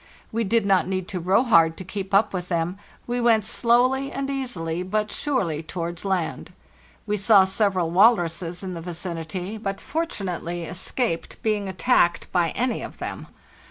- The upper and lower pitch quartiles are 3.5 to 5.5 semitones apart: Yes, average, 4.5 semitones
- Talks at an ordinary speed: Yes, average, 165 wpm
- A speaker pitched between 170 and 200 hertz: Yes, high, 190 Hz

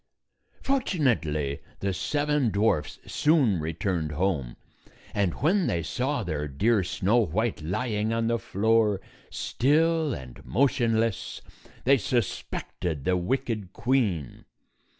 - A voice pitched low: Yes, low, 105 Hz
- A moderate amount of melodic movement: No, wide, 6.7 semitones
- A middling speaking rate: No, slow, 110 wpm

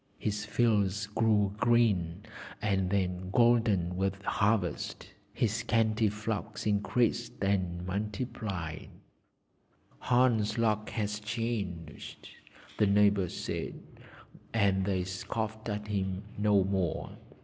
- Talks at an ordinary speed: No, slow, 100 wpm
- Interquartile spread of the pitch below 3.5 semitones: Yes, narrow, 2.6 semitones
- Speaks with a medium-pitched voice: No, low, 105 Hz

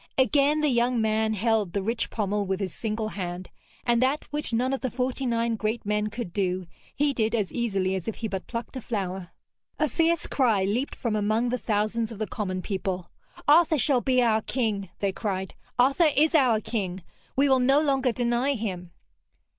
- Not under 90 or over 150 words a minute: No, average, 195 wpm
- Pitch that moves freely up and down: No, average, 4.2 semitones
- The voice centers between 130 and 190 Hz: No, high, 225 Hz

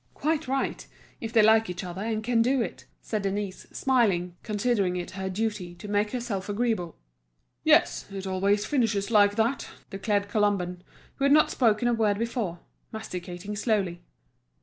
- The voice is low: No, high, 210 Hz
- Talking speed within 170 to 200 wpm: No, average, 160 wpm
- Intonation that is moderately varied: Yes, average, 3.2 semitones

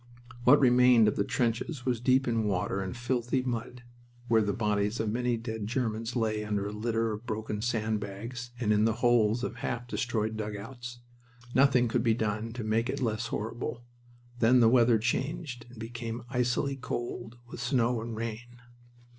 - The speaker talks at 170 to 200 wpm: Yes, average, 175 wpm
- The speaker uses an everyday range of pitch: No, narrow, 2.0 semitones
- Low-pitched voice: Yes, low, 115 Hz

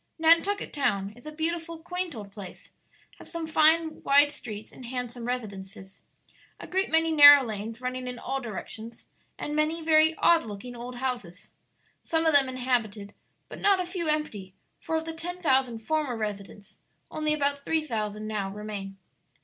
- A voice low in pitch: No, very high, 260 Hz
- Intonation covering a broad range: Yes, wide, 6.8 semitones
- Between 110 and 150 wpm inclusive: No, average, 165 wpm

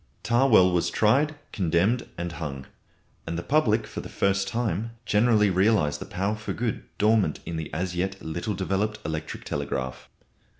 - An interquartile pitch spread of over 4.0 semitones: Yes, average, 4.4 semitones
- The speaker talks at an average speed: Yes, average, 160 wpm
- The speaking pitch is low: Yes, very low, 95 Hz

